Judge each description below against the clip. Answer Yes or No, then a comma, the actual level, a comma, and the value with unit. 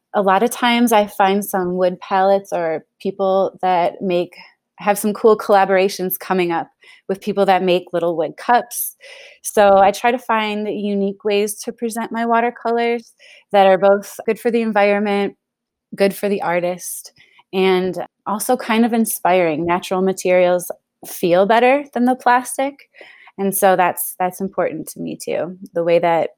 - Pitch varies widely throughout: No, average, 3.8 semitones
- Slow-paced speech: No, average, 160 wpm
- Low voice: No, high, 200 Hz